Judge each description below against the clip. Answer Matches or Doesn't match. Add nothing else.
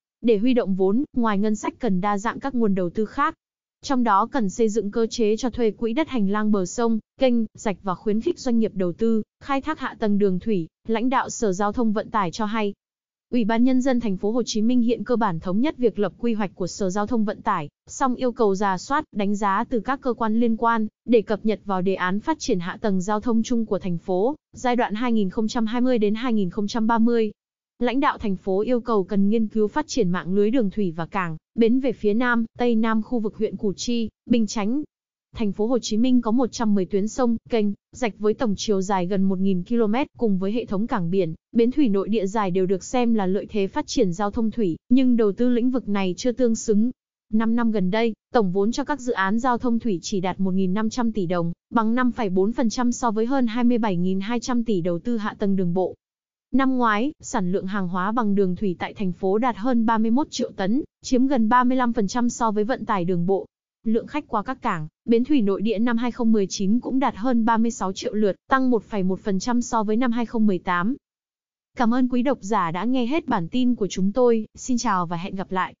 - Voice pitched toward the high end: Matches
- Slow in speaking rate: Doesn't match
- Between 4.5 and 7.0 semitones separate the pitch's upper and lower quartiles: Doesn't match